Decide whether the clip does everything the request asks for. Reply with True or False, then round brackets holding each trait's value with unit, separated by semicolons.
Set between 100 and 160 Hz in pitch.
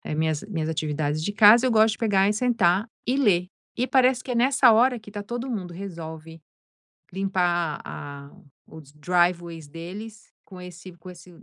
False (185 Hz)